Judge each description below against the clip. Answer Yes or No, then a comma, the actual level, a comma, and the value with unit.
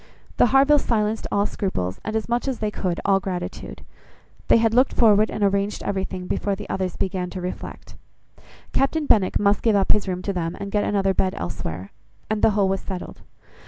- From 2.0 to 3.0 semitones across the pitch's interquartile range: Yes, narrow, 2.6 semitones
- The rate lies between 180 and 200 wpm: Yes, average, 195 wpm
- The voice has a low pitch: No, high, 200 Hz